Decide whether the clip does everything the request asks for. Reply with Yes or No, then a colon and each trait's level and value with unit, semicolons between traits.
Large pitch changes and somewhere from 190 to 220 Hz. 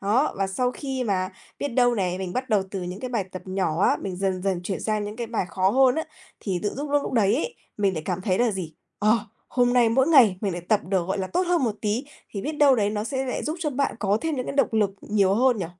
No: average, 5.0 semitones; high, 215 Hz